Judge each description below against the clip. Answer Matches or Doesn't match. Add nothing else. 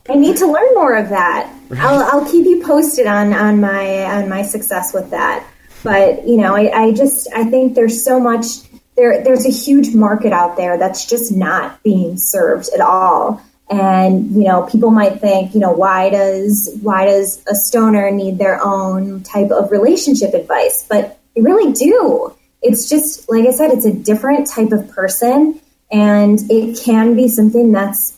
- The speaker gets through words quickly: Doesn't match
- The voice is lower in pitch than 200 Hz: Doesn't match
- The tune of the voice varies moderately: Matches